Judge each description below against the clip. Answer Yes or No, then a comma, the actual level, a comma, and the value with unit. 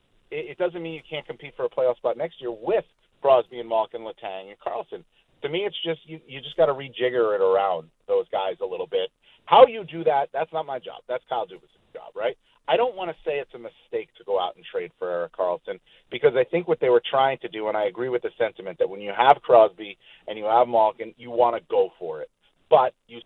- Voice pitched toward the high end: Yes, high, 240 Hz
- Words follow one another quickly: Yes, fast, 245 wpm